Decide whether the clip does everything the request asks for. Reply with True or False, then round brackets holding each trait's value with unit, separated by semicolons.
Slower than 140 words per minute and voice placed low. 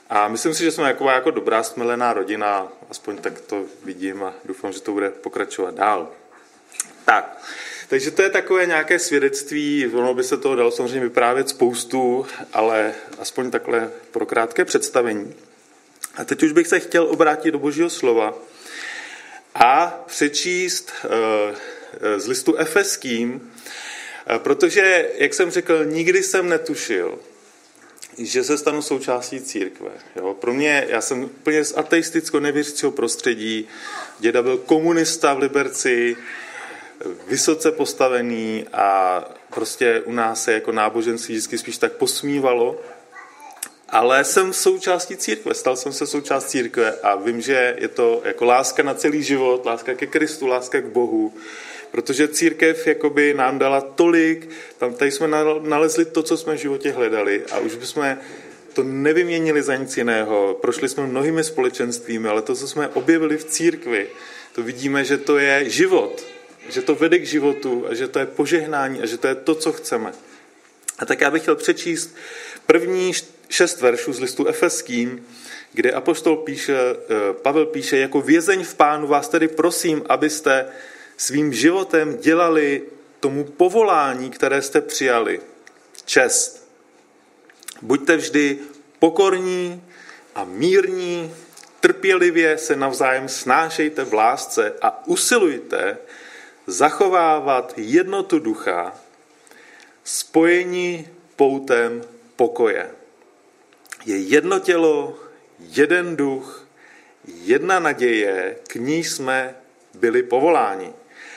False (130 wpm; 165 Hz)